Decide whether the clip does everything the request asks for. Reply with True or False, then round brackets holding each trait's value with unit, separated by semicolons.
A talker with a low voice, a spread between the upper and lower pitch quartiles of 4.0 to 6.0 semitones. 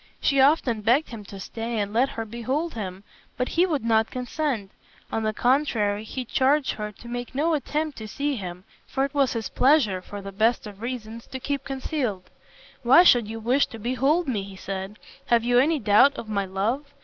False (235 Hz; 4.5 semitones)